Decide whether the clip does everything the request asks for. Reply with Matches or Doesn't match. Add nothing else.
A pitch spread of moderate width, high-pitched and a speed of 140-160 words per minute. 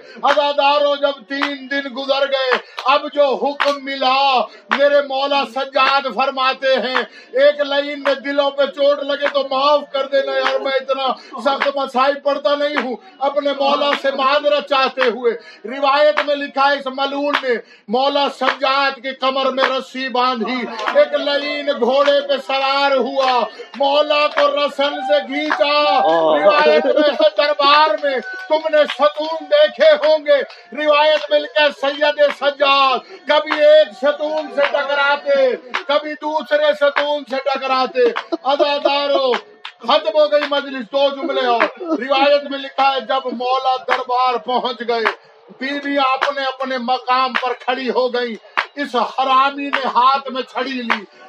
Doesn't match